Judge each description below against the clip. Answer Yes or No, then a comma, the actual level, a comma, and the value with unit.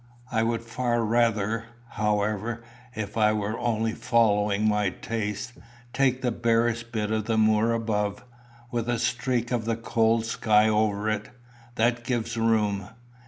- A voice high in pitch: No, low, 110 Hz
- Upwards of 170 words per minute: No, average, 145 wpm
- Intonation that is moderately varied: No, narrow, 1.7 semitones